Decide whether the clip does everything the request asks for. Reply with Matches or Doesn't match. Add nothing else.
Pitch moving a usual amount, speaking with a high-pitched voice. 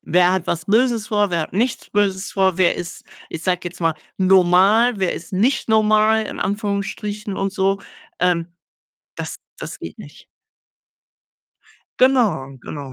Matches